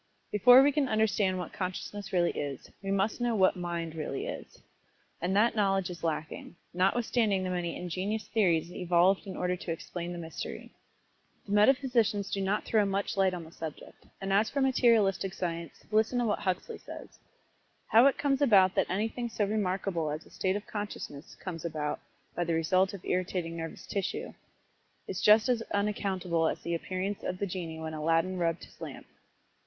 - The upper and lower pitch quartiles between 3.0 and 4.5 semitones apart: Yes, average, 3.5 semitones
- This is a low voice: No, high, 190 Hz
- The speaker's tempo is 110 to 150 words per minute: No, average, 180 wpm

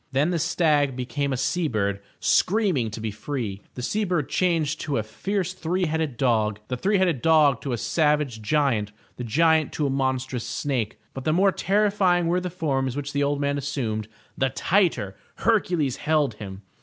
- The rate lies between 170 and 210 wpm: Yes, average, 190 wpm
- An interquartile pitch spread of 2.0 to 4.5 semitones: No, average, 5.3 semitones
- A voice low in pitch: No, medium, 145 Hz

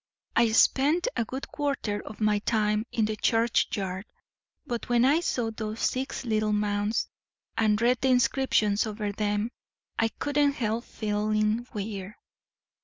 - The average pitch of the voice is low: No, high, 220 Hz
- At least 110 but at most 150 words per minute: Yes, average, 140 wpm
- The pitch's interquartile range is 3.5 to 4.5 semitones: No, average, 2.7 semitones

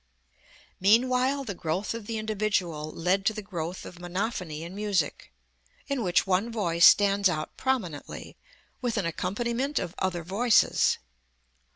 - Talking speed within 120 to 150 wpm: Yes, average, 140 wpm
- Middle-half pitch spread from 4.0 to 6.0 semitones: Yes, average, 4.6 semitones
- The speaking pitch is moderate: No, high, 200 Hz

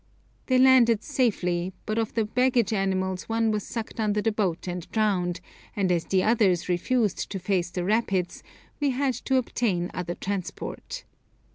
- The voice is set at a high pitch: Yes, high, 210 Hz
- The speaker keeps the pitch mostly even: No, average, 4.3 semitones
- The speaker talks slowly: No, average, 160 wpm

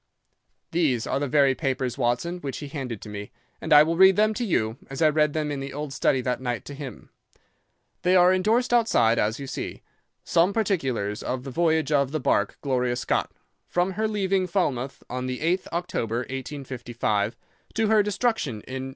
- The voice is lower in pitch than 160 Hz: Yes, medium, 140 Hz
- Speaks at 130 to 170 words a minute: No, average, 195 wpm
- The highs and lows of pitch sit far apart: Yes, wide, 6.0 semitones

